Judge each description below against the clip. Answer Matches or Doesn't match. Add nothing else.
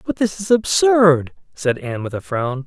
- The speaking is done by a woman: Doesn't match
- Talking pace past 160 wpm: Matches